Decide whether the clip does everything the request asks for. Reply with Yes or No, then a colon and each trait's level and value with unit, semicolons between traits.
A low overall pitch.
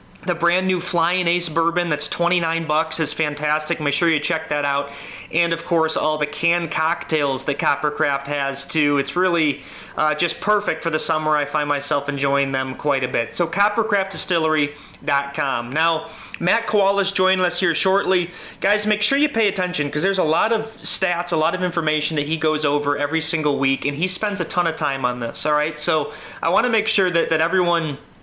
No: medium, 160 Hz